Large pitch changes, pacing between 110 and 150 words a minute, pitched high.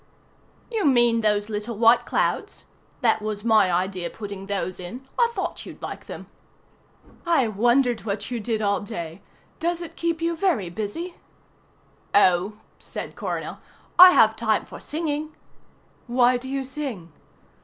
Yes: wide, 6.3 semitones; average, 145 wpm; high, 230 Hz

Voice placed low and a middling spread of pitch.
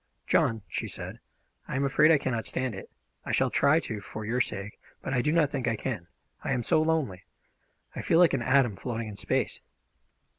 Yes: low, 125 Hz; average, 4.3 semitones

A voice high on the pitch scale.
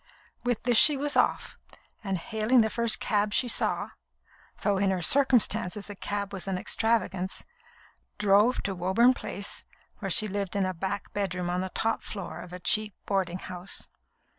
Yes: high, 200 Hz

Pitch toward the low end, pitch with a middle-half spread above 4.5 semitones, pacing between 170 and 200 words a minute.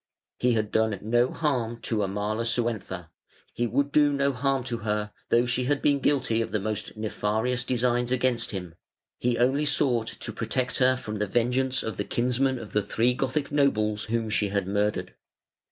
No: low, 120 Hz; average, 3.1 semitones; average, 180 wpm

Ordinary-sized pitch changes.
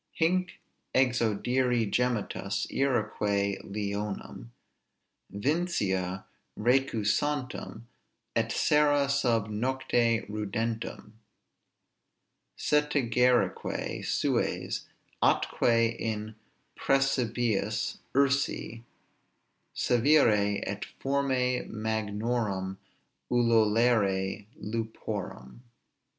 Yes: average, 3.9 semitones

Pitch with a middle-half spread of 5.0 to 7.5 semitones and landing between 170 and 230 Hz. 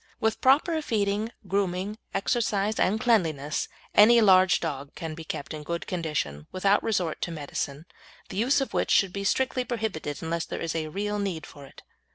Yes: average, 5.3 semitones; high, 190 Hz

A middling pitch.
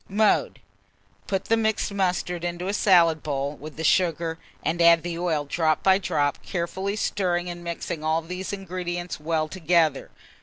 Yes: medium, 175 Hz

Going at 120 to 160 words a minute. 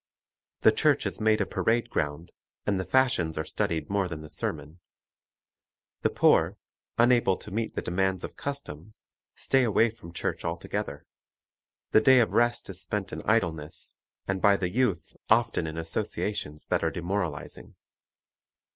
Yes: average, 155 wpm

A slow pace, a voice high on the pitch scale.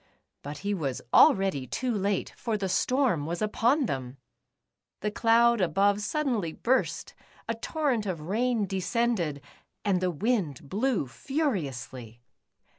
Yes: slow, 130 wpm; high, 200 Hz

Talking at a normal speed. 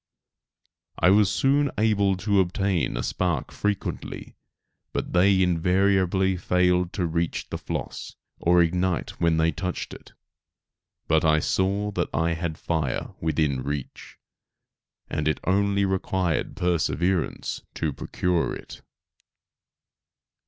No: slow, 120 wpm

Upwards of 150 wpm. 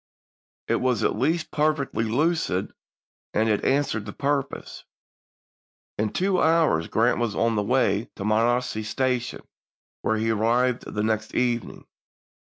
No: slow, 135 wpm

